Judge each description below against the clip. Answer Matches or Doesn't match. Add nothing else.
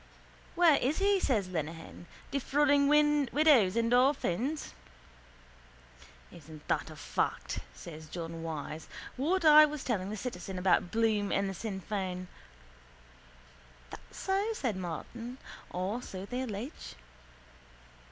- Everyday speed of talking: Doesn't match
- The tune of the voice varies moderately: Doesn't match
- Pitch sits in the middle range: Doesn't match